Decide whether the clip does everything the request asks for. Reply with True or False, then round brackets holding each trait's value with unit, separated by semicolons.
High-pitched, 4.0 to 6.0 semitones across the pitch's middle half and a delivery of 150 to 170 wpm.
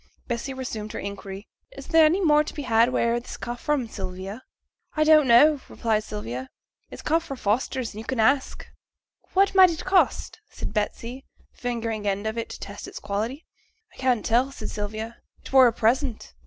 False (240 Hz; 4.4 semitones; 195 wpm)